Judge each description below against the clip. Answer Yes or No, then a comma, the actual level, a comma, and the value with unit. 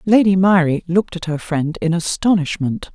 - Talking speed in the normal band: Yes, average, 165 wpm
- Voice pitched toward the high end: No, medium, 175 Hz